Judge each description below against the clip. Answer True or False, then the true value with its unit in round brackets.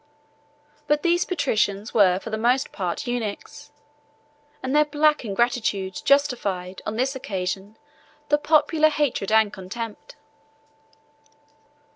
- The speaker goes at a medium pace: False (110 wpm)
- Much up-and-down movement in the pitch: True (6.5 semitones)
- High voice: True (235 Hz)